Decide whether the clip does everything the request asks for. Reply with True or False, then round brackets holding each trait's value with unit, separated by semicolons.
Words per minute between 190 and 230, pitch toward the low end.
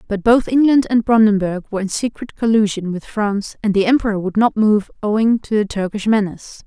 False (200 wpm; 210 Hz)